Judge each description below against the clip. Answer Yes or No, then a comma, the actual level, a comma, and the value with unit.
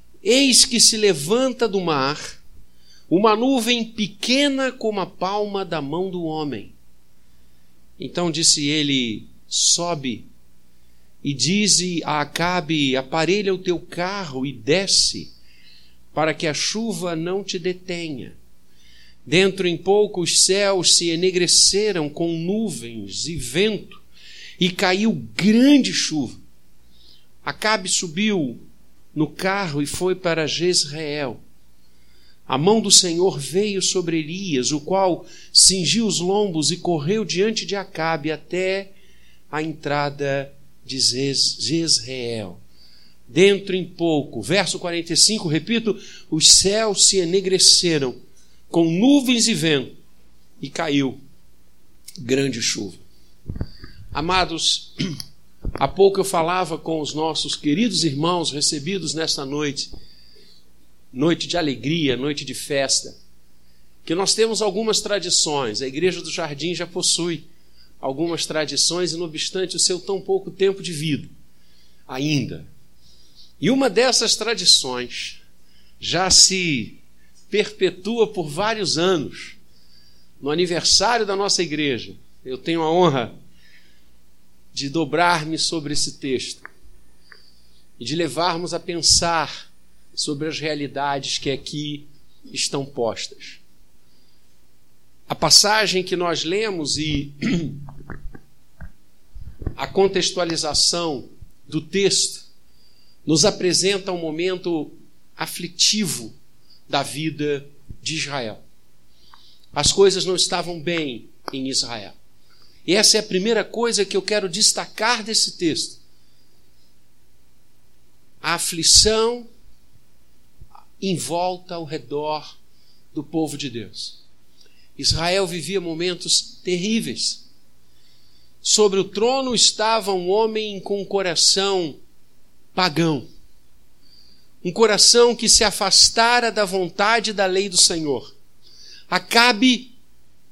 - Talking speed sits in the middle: No, slow, 110 wpm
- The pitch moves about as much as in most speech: No, wide, 7.6 semitones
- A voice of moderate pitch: Yes, medium, 160 Hz